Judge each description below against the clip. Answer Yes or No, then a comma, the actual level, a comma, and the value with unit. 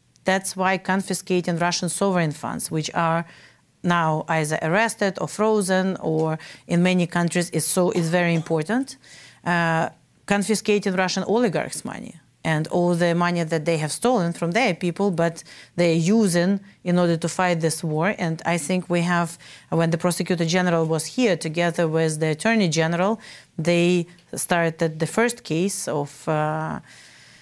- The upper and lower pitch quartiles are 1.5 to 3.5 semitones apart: Yes, narrow, 2.5 semitones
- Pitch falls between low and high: Yes, medium, 175 Hz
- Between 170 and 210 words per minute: No, average, 155 wpm